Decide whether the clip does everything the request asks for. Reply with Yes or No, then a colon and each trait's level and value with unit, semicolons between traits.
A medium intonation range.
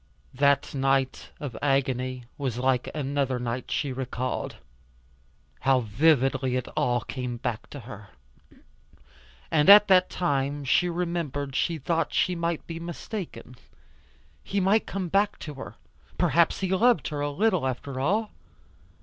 Yes: average, 4.9 semitones